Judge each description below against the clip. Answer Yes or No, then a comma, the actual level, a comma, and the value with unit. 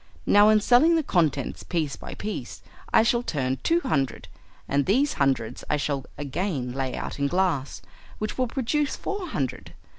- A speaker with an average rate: Yes, average, 170 wpm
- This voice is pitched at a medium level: Yes, medium, 175 Hz